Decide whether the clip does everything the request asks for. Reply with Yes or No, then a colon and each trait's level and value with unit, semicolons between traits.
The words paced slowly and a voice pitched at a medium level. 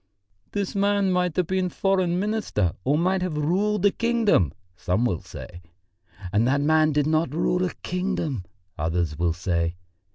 No: average, 160 wpm; medium, 165 Hz